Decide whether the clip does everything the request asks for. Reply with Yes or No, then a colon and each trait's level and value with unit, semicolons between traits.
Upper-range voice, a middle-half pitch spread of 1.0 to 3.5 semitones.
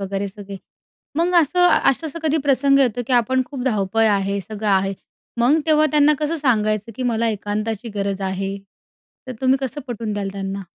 No: high, 225 Hz; wide, 5.6 semitones